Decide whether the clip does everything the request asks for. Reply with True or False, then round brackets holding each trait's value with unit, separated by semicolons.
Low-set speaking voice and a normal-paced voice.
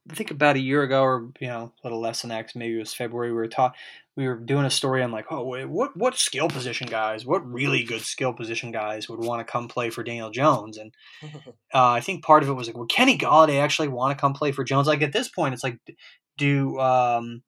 False (130 Hz; 260 wpm)